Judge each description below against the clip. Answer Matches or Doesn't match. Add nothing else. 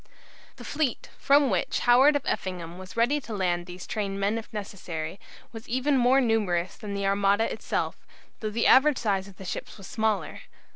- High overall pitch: Matches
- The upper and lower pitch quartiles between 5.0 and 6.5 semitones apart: Doesn't match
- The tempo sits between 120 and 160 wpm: Doesn't match